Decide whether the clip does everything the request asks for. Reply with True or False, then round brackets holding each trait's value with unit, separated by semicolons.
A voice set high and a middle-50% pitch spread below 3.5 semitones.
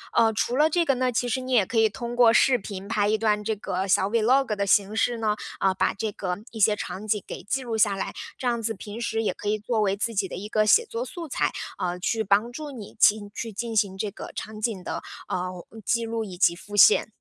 True (215 Hz; 2.8 semitones)